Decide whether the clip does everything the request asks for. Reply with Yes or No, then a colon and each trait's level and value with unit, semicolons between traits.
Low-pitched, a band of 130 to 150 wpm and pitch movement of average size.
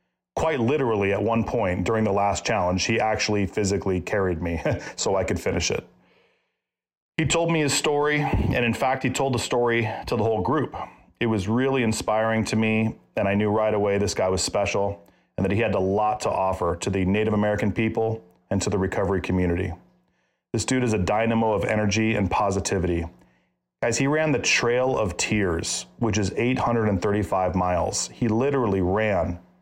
No: low, 105 Hz; average, 185 wpm; average, 3.4 semitones